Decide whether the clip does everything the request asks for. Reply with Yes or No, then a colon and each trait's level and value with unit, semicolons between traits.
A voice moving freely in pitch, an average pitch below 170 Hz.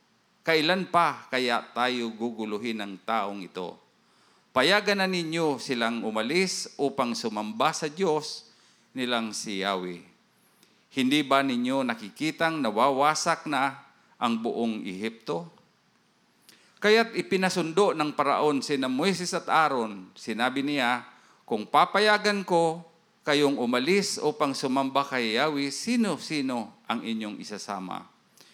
Yes: wide, 6.1 semitones; medium, 140 Hz